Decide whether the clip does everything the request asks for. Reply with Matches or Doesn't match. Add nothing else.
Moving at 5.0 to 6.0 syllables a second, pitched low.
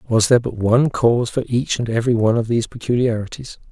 Doesn't match